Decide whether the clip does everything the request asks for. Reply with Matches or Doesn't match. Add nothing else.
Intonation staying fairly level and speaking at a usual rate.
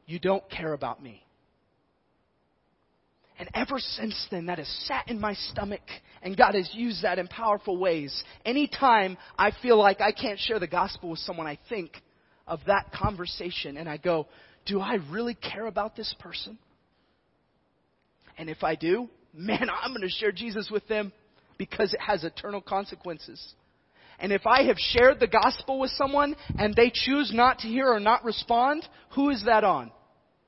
Doesn't match